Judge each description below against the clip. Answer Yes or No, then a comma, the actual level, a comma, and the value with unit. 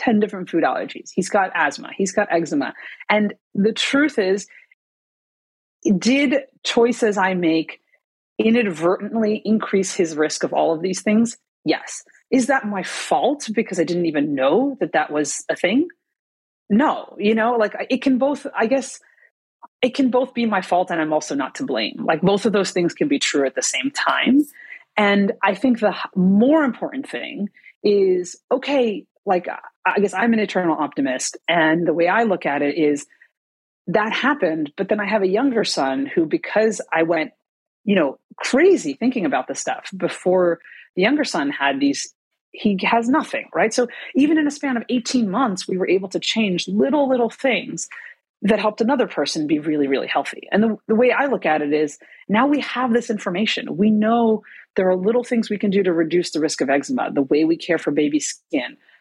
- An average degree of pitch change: No, wide, 6.5 semitones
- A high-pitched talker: Yes, high, 215 Hz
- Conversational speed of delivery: Yes, average, 190 wpm